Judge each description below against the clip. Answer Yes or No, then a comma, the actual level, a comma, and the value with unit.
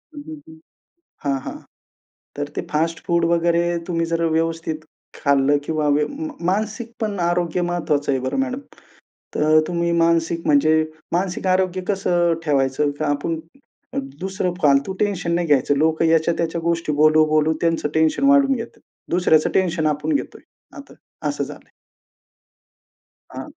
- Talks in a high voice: No, medium, 165 Hz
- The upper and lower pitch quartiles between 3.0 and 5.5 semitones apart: No, narrow, 2.6 semitones